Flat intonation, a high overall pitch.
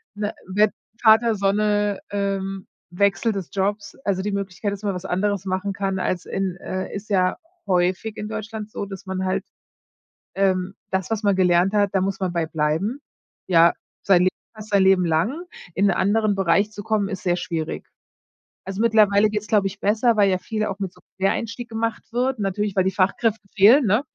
Yes: narrow, 2.2 semitones; high, 200 Hz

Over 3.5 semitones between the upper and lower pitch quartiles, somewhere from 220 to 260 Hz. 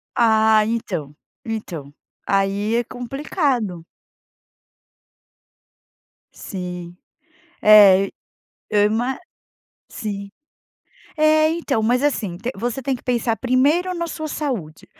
Yes: average, 5.1 semitones; high, 225 Hz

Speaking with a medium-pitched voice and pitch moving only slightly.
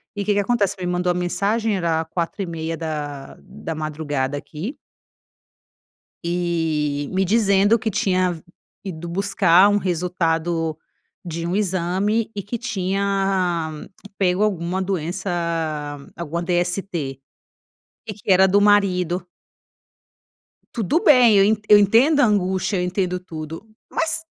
No: medium, 180 Hz; average, 3.3 semitones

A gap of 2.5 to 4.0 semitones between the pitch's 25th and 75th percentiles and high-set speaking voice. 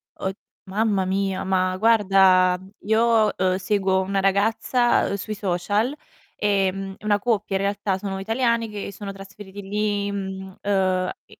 No: narrow, 1.7 semitones; high, 195 Hz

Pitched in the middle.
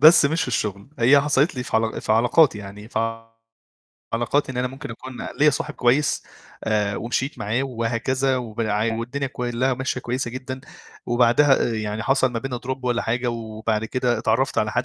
No: low, 120 Hz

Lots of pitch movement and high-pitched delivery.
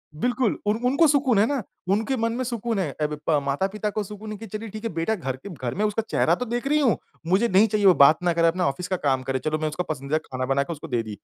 Yes: wide, 6.8 semitones; high, 195 Hz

